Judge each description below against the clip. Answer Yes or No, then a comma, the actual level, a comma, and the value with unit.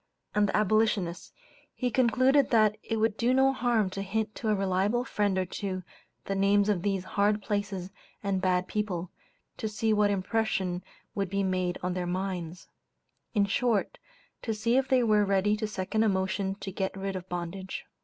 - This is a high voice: Yes, high, 200 Hz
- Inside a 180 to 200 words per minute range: Yes, average, 185 wpm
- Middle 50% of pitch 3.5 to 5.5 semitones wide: No, narrow, 2.5 semitones